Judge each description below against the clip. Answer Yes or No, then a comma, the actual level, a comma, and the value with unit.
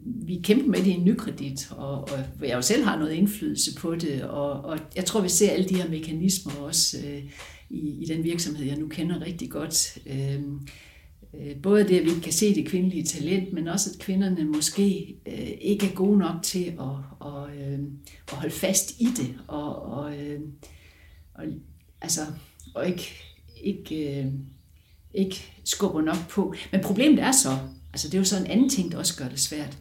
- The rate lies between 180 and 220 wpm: Yes, average, 195 wpm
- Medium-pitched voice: Yes, medium, 160 Hz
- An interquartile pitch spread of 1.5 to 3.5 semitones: No, average, 5.1 semitones